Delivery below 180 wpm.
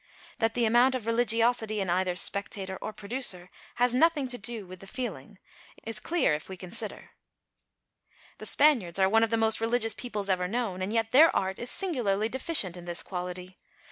No: average, 185 wpm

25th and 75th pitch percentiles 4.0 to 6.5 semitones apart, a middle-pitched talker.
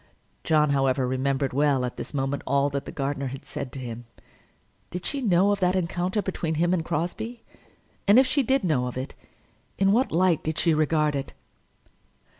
Yes: average, 5.2 semitones; medium, 155 Hz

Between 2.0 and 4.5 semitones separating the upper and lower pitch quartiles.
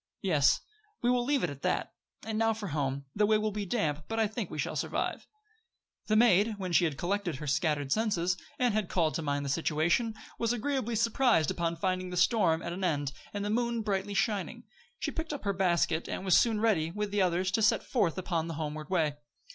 No: average, 5.2 semitones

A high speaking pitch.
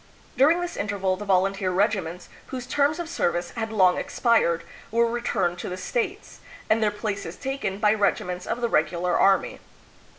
Yes: high, 205 Hz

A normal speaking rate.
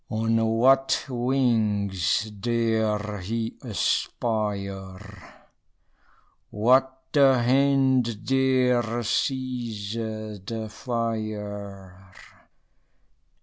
No: slow, 60 wpm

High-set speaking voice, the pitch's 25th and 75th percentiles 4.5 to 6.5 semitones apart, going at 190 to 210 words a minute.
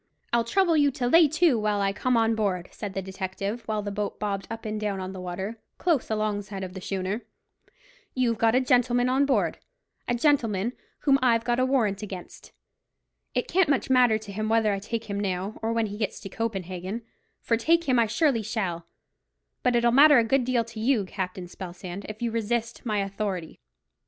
No: high, 220 Hz; average, 3.7 semitones; average, 200 wpm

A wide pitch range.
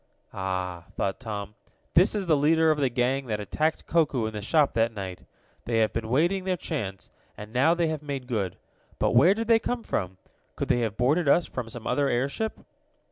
Yes: wide, 6.8 semitones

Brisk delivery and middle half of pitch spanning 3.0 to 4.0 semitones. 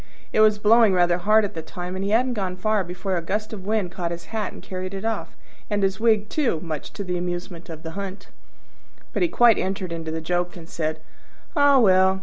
Yes: fast, 230 wpm; average, 3.4 semitones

